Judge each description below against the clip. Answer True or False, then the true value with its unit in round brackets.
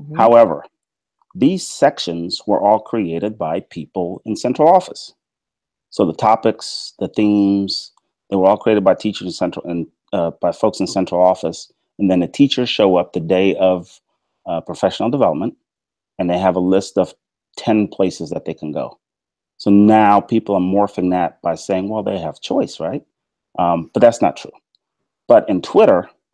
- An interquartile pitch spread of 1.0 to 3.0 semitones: True (2.6 semitones)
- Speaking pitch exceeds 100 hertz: False (95 Hz)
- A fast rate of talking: False (175 wpm)